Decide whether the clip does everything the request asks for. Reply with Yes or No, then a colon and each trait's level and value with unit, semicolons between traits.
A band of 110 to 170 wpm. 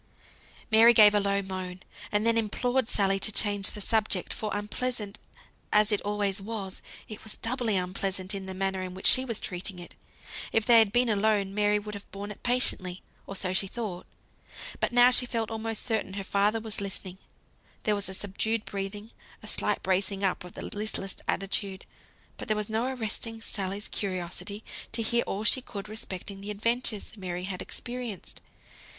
No: average, 180 wpm